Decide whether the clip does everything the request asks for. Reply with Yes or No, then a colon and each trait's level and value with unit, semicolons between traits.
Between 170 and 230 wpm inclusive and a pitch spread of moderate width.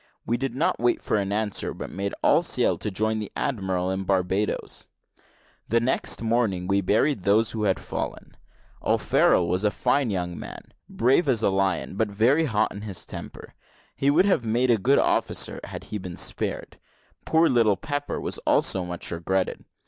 Yes: average, 180 wpm; average, 4.1 semitones